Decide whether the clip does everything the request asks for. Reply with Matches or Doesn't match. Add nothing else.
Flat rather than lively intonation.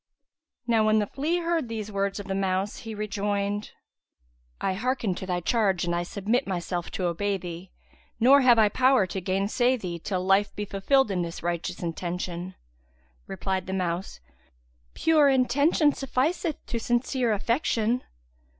Doesn't match